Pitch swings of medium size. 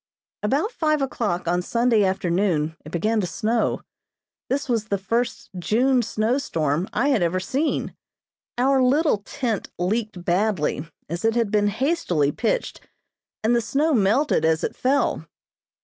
No: wide, 6.3 semitones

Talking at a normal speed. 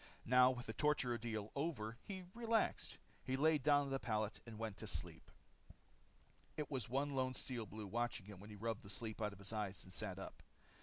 No: fast, 210 wpm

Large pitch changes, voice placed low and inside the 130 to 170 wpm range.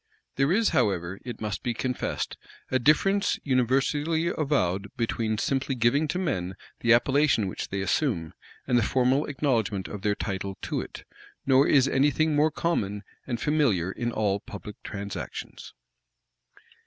Yes: wide, 6.2 semitones; low, 120 Hz; average, 150 wpm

